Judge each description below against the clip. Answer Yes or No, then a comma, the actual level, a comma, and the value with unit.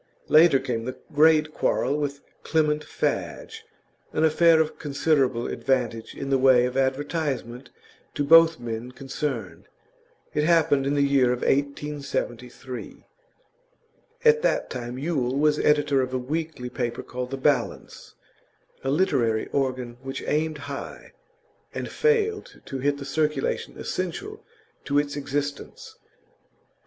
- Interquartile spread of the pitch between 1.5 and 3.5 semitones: Yes, average, 3.1 semitones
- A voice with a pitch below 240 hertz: Yes, medium, 140 Hz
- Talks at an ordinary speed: No, slow, 130 wpm